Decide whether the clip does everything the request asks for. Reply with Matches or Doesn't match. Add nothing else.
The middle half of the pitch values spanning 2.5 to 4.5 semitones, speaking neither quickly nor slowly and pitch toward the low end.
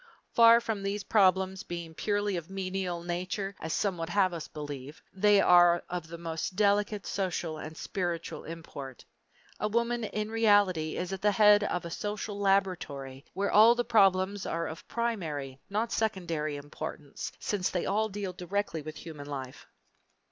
Doesn't match